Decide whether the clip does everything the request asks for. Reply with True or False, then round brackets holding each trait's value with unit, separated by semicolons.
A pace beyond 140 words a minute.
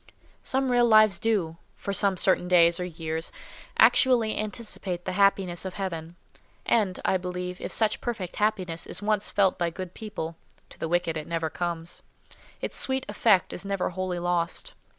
True (160 wpm)